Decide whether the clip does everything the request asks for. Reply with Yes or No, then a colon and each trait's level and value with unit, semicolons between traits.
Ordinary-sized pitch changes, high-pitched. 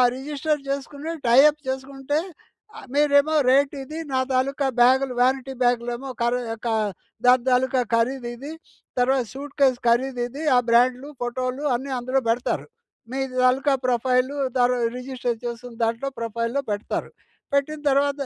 No: narrow, 2.2 semitones; very high, 260 Hz